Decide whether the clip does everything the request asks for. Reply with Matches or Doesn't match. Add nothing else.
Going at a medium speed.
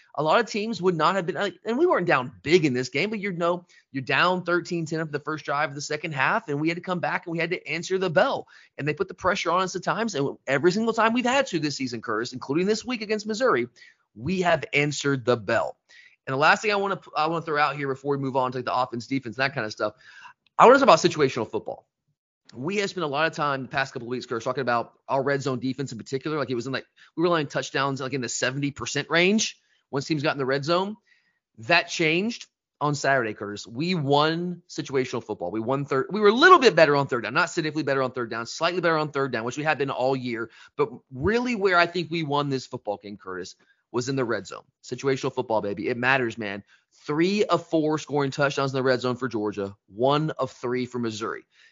Doesn't match